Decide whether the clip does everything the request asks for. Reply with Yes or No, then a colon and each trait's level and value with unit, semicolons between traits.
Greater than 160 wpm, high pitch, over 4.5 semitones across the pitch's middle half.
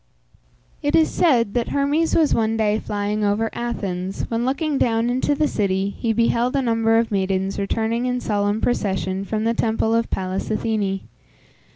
No: average, 170 wpm; high, 225 Hz; average, 3.0 semitones